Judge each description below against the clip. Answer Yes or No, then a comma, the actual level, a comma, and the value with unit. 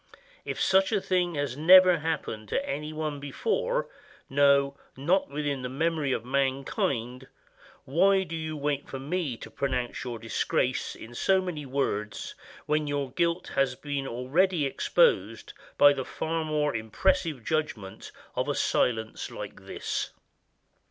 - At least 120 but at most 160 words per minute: Yes, average, 145 wpm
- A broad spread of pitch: No, average, 4.2 semitones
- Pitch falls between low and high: Yes, medium, 145 Hz